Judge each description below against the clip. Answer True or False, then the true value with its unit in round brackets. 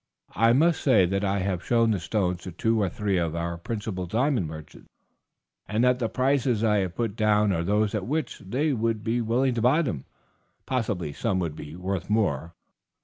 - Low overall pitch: True (105 Hz)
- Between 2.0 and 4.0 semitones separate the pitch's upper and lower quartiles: False (4.5 semitones)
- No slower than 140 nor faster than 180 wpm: False (200 wpm)